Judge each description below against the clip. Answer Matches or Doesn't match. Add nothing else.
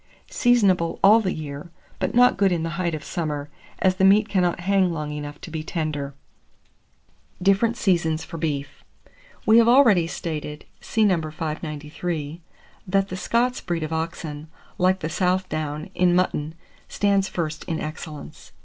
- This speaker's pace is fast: Doesn't match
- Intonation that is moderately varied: Matches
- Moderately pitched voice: Matches